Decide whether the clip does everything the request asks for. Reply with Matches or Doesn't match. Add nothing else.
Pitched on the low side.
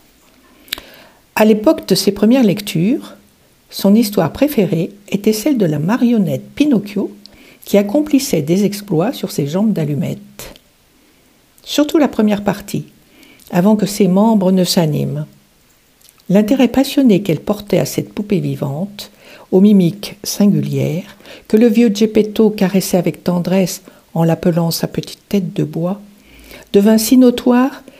Doesn't match